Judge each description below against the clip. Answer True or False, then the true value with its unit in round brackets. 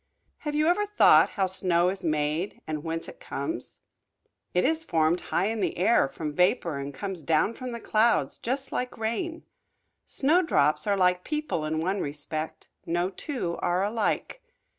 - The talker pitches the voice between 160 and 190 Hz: True (185 Hz)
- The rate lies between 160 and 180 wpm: True (165 wpm)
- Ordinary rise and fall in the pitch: False (7.2 semitones)